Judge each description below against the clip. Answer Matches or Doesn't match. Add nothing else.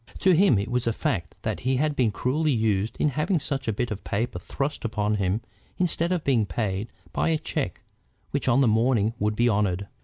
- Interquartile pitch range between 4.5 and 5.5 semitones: Matches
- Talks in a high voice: Doesn't match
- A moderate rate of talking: Doesn't match